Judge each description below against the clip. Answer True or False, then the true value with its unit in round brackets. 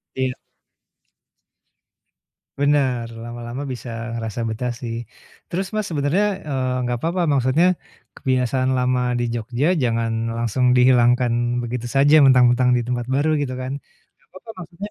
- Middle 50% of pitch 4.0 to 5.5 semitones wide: False (2.8 semitones)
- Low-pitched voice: True (125 Hz)